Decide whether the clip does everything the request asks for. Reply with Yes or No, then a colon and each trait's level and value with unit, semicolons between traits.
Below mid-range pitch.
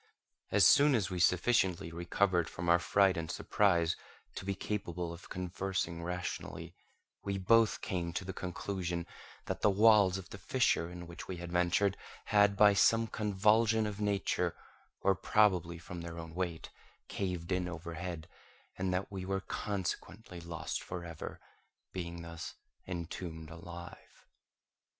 Yes: very low, 90 Hz